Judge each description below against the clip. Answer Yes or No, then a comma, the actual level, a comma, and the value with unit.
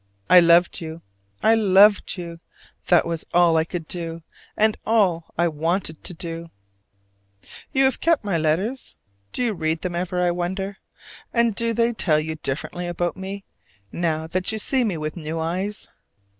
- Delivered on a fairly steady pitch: No, average, 3.7 semitones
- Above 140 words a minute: Yes, average, 170 wpm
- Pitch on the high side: No, medium, 175 Hz